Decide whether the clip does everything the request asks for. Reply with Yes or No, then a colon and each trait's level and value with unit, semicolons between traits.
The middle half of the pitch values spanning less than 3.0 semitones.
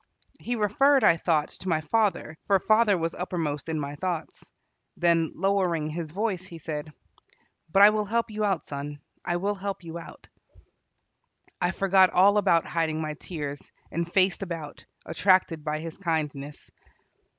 No: average, 3.9 semitones